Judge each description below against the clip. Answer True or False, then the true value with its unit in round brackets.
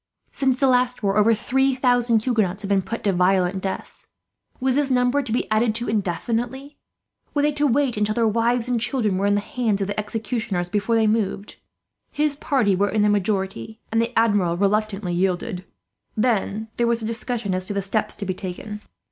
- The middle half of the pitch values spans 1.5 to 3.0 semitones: False (3.5 semitones)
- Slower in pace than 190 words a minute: False (200 wpm)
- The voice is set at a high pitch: True (220 Hz)